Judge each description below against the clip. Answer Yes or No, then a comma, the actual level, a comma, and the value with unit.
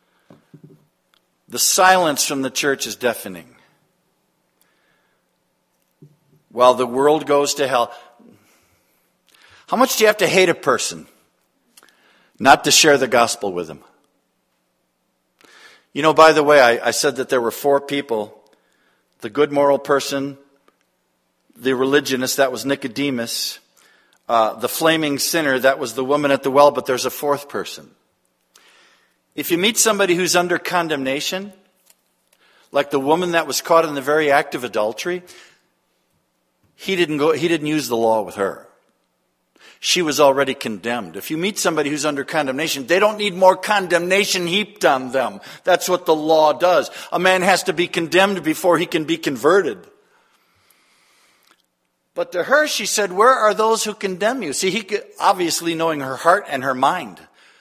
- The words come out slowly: No, average, 160 wpm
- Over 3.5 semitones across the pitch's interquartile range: Yes, average, 5.1 semitones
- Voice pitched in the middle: Yes, medium, 155 Hz